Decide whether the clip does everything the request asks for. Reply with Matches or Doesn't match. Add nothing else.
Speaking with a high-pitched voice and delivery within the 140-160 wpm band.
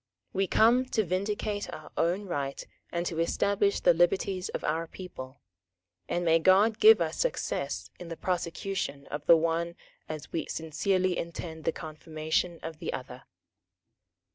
Doesn't match